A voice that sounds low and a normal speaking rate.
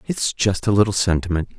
Yes: low, 100 Hz; average, 190 wpm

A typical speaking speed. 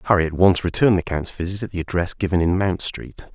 No: fast, 250 wpm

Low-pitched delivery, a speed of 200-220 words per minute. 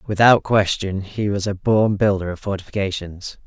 No: low, 100 Hz; average, 155 wpm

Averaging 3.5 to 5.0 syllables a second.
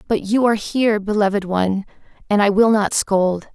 No: 5.6 syllables/s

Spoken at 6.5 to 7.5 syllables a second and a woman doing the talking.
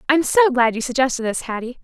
Yes: 6.6 syllables/s; female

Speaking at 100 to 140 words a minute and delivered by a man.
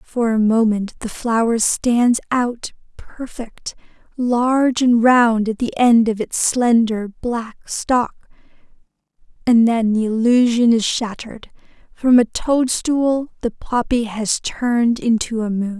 No: slow, 135 wpm; female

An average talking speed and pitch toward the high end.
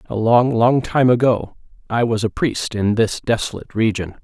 No: average, 185 wpm; low, 115 Hz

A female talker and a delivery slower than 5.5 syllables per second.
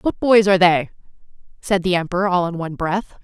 No: female; 6.1 syllables/s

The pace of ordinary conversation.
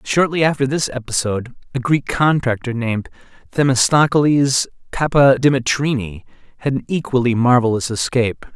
No: slow, 105 wpm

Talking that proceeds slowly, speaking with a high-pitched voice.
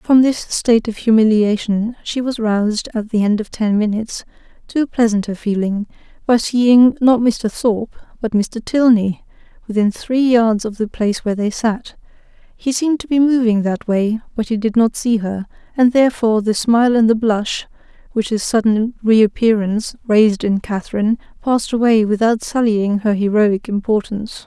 No: average, 170 wpm; high, 220 Hz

